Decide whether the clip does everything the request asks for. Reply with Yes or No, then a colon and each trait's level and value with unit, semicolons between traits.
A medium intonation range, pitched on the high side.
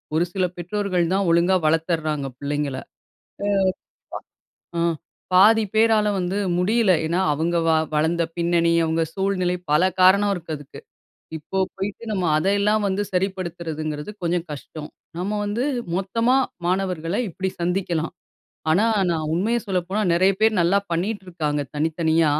No: average, 3.3 semitones; medium, 180 Hz